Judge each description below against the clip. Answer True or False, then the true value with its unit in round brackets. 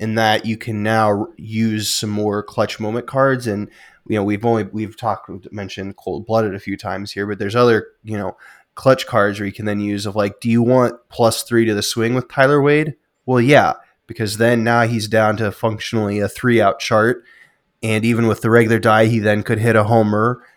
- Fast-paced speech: True (220 wpm)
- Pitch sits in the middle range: False (110 Hz)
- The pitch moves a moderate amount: False (2.1 semitones)